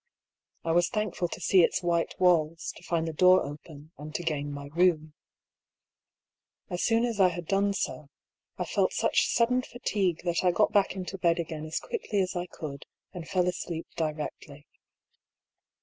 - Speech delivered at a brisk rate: No, average, 175 wpm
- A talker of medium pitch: Yes, medium, 175 Hz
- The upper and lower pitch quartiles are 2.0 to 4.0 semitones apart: Yes, average, 2.9 semitones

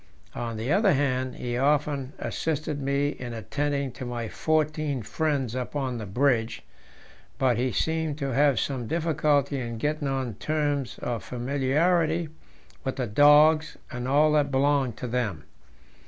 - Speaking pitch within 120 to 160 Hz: Yes, medium, 140 Hz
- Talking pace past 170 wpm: No, average, 150 wpm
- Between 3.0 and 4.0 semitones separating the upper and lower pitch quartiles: Yes, average, 3.3 semitones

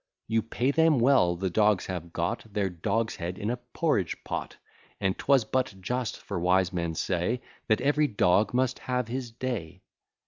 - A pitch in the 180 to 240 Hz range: No, low, 110 Hz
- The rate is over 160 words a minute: Yes, average, 175 wpm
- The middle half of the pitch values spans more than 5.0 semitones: Yes, wide, 5.6 semitones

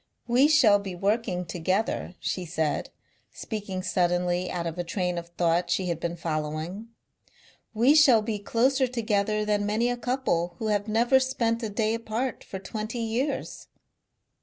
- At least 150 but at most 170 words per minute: Yes, average, 160 wpm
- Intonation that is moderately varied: Yes, average, 4.6 semitones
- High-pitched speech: Yes, high, 210 Hz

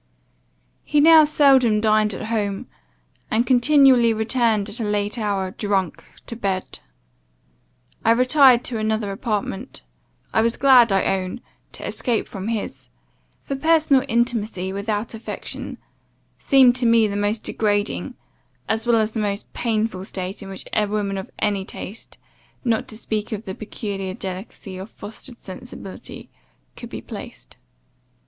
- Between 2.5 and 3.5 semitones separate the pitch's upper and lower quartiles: Yes, average, 3.0 semitones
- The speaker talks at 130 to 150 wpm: Yes, average, 145 wpm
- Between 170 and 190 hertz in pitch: No, high, 215 Hz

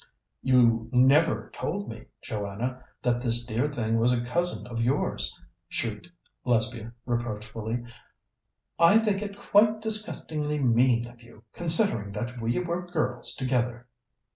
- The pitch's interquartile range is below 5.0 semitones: No, wide, 5.6 semitones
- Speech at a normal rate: No, slow, 130 wpm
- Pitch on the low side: Yes, low, 125 Hz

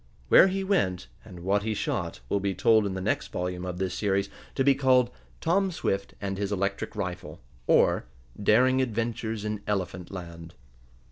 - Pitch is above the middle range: No, low, 100 Hz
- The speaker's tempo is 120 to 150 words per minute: No, average, 175 wpm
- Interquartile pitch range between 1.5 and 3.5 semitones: No, average, 4.3 semitones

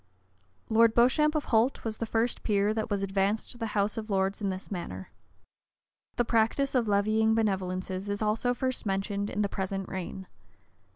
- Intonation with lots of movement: No, narrow, 2.6 semitones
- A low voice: No, high, 210 Hz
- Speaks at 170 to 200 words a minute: Yes, average, 175 wpm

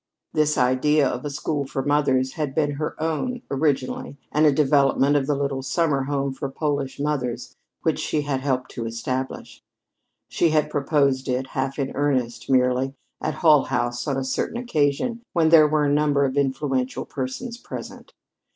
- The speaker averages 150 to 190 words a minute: Yes, average, 170 wpm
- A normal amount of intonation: No, narrow, 2.3 semitones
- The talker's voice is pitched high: No, medium, 140 Hz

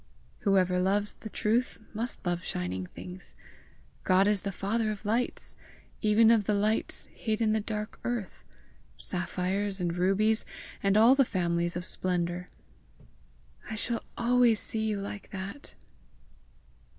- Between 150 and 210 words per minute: No, average, 140 wpm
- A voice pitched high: Yes, high, 205 Hz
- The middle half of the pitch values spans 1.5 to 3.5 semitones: Yes, average, 3.1 semitones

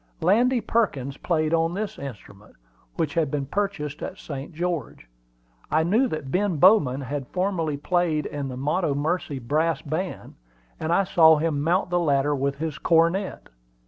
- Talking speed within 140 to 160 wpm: Yes, average, 155 wpm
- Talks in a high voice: No, medium, 160 Hz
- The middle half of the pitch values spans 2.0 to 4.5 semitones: Yes, average, 4.0 semitones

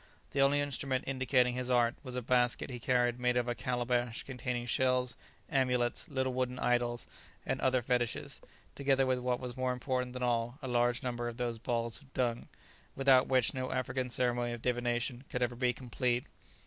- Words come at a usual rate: Yes, average, 185 wpm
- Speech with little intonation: Yes, narrow, 1.0 semitones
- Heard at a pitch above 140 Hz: No, low, 125 Hz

